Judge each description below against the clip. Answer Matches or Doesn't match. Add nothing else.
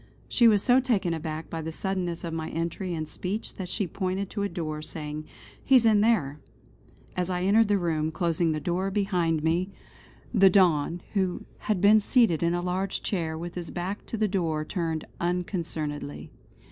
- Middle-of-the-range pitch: Matches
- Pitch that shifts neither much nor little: Matches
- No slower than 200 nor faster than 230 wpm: Doesn't match